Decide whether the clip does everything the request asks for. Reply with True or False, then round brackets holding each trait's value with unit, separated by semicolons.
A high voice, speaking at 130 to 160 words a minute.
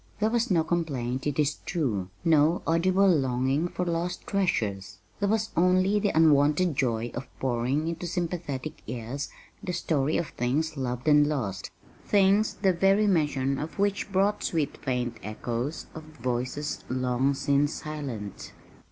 False (150 Hz; 145 wpm)